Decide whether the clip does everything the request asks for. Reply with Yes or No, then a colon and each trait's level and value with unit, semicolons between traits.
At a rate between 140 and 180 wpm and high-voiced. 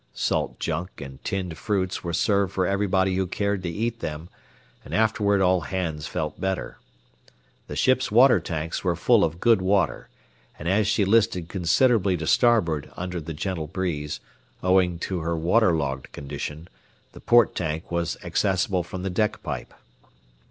No: average, 160 wpm; very low, 90 Hz